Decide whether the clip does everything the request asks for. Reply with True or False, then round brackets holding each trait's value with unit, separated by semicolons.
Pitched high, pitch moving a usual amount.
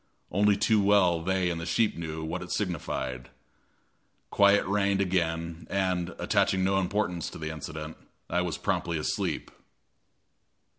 False (90 Hz; 3.1 semitones)